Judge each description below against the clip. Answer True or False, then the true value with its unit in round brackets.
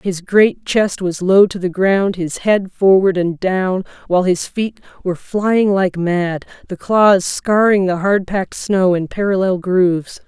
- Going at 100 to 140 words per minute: False (175 wpm)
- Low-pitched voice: False (190 Hz)